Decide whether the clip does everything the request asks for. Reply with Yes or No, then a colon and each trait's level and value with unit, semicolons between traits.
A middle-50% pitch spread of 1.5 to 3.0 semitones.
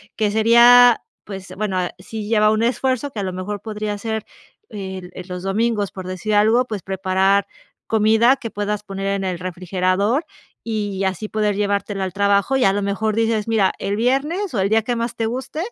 Yes: average, 2.7 semitones